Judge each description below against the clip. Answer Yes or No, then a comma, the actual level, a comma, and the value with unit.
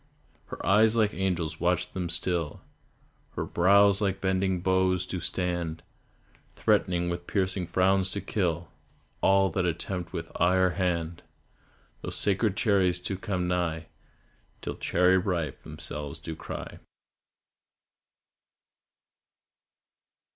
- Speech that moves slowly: Yes, slow, 115 wpm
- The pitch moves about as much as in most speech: No, narrow, 1.8 semitones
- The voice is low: Yes, very low, 90 Hz